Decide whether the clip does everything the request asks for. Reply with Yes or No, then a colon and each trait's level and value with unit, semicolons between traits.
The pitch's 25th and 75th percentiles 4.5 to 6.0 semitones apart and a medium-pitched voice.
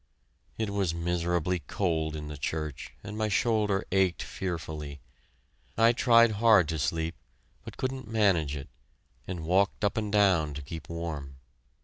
No: average, 4.8 semitones; very low, 90 Hz